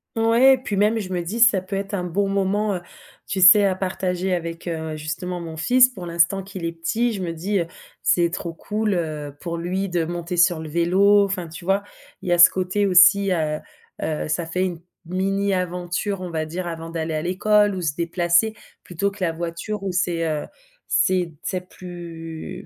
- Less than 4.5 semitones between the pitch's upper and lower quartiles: Yes, average, 2.8 semitones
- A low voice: No, medium, 180 Hz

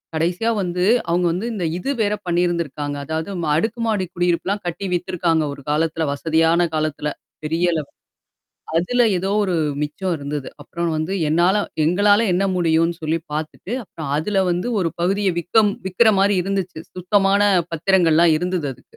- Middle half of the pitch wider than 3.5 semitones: No, average, 3.2 semitones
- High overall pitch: No, medium, 175 Hz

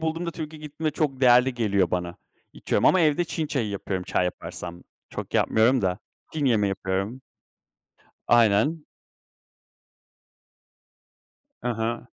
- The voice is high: No, low, 120 Hz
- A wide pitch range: Yes, wide, 7.3 semitones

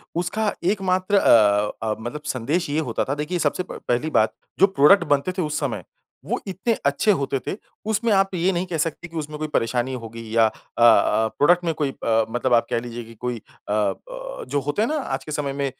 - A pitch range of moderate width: No, wide, 7.0 semitones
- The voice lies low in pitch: No, medium, 145 Hz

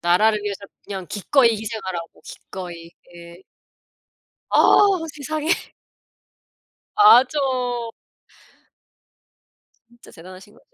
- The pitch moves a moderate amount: No, wide, 6.5 semitones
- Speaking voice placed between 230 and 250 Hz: No, high, 220 Hz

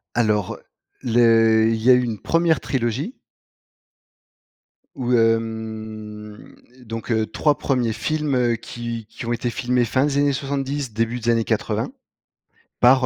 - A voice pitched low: Yes, low, 120 Hz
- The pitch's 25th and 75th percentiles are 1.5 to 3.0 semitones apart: Yes, narrow, 2.6 semitones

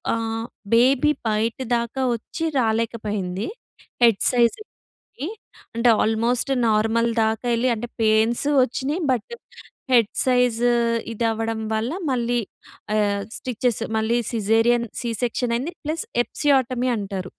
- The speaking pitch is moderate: No, high, 230 Hz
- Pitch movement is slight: Yes, narrow, 2.0 semitones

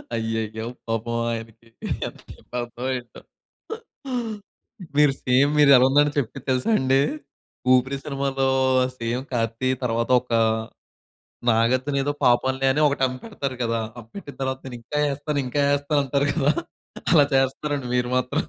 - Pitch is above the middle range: No, low, 130 Hz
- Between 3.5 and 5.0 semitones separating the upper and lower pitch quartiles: No, average, 3.1 semitones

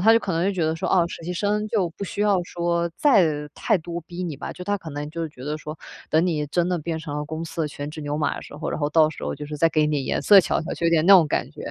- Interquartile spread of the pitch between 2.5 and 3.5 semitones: Yes, average, 3.1 semitones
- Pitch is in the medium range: Yes, medium, 165 Hz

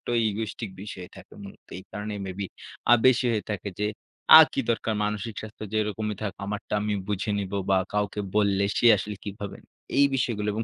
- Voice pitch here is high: No, low, 105 Hz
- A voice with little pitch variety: Yes, narrow, 1.3 semitones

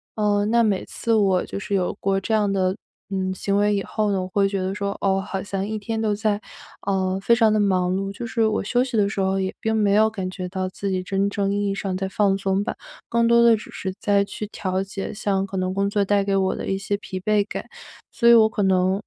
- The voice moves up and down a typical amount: No, narrow, 1.7 semitones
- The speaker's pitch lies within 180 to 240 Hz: Yes, high, 200 Hz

